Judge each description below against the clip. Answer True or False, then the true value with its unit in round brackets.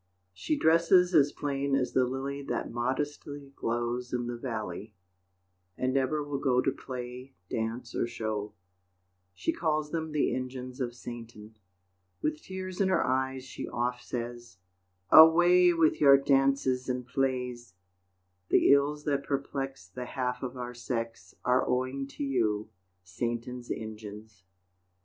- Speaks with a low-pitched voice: True (130 Hz)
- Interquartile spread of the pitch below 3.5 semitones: True (2.8 semitones)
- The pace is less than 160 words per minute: True (140 wpm)